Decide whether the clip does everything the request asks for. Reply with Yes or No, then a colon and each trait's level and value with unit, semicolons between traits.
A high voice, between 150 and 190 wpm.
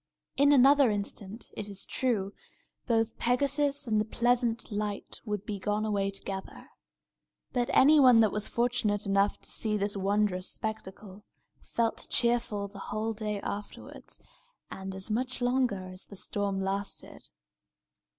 No: high, 210 Hz; average, 140 wpm